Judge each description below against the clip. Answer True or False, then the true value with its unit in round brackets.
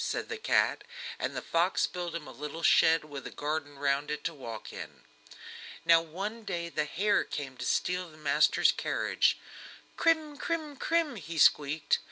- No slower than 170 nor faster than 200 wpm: True (175 wpm)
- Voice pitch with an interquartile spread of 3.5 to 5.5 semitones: True (5.1 semitones)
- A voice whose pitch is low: False (165 Hz)